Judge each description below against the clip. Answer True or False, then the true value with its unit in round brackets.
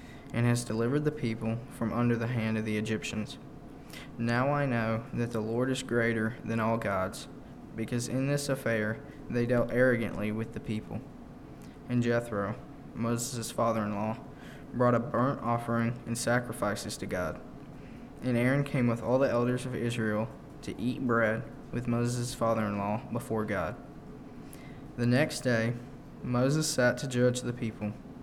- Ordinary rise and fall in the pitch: False (1.9 semitones)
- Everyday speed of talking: True (160 wpm)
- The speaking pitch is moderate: False (120 Hz)